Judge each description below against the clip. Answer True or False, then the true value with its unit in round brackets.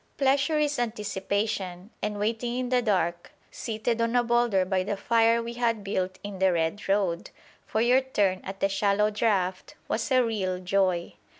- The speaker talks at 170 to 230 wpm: True (175 wpm)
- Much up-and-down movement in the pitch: False (3.8 semitones)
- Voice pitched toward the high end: True (210 Hz)